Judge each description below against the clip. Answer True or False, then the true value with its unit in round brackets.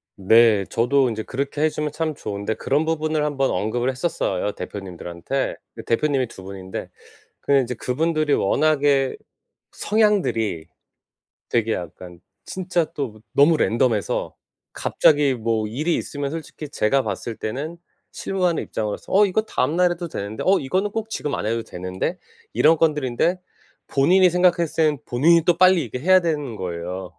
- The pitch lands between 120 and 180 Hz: True (140 Hz)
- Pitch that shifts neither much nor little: False (6.8 semitones)